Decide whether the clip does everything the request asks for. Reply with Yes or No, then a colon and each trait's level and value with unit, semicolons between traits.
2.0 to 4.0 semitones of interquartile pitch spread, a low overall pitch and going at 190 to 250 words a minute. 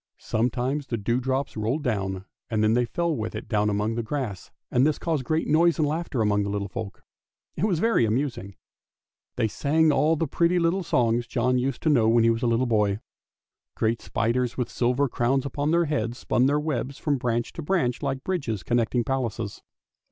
No: average, 4.5 semitones; low, 125 Hz; average, 195 wpm